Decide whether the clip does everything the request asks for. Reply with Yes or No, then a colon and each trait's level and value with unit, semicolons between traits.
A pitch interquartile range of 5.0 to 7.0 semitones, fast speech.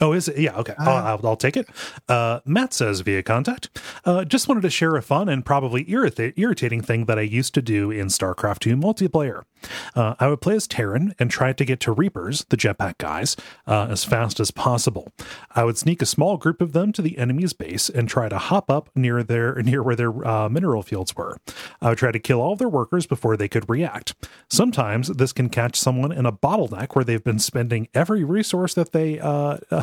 Yes: wide, 5.6 semitones; fast, 225 wpm